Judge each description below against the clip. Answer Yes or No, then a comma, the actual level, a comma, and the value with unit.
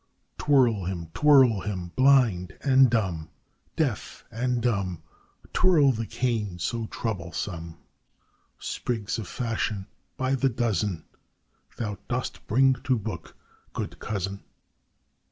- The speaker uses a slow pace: Yes, slow, 110 wpm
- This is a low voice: Yes, low, 110 Hz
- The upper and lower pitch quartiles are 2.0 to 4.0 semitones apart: No, average, 5.0 semitones